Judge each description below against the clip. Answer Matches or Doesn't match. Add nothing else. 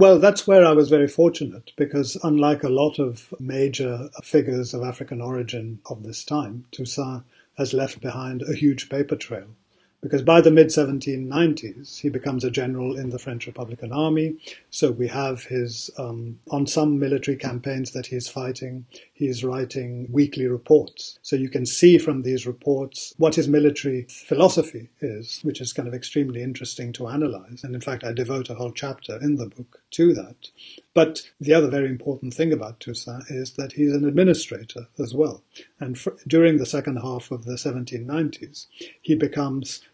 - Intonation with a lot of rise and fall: Doesn't match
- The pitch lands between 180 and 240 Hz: Doesn't match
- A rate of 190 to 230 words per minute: Doesn't match